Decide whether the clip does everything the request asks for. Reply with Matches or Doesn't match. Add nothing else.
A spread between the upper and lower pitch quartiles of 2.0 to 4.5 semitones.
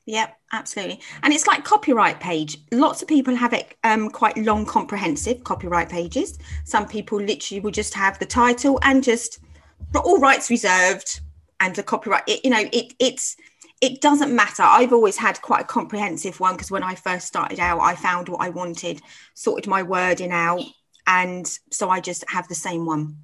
Doesn't match